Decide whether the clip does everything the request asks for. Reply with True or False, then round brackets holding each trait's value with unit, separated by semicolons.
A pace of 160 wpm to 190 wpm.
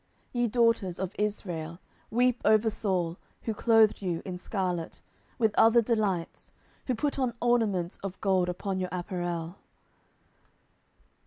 False (135 wpm)